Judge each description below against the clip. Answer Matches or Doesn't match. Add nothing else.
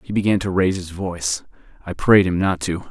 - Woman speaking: Doesn't match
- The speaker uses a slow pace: Doesn't match